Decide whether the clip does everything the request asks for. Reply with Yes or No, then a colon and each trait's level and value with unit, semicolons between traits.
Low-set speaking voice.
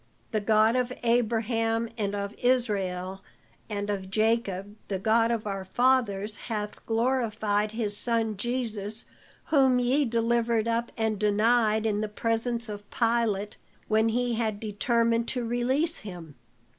No: high, 225 Hz